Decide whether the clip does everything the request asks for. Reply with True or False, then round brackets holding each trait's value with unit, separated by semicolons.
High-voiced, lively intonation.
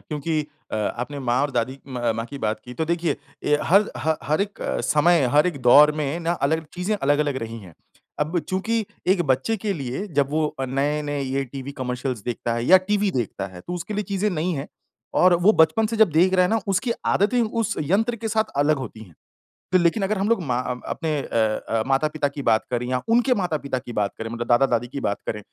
False (150 Hz; 6.6 semitones)